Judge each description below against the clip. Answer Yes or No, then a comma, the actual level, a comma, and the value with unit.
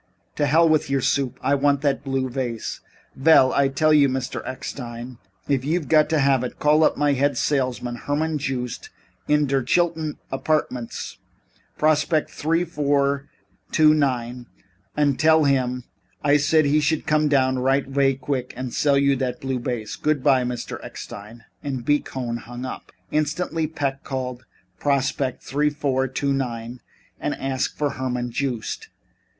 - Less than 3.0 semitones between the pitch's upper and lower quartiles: Yes, narrow, 2.6 semitones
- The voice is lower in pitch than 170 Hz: Yes, medium, 140 Hz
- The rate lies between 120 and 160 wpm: Yes, average, 150 wpm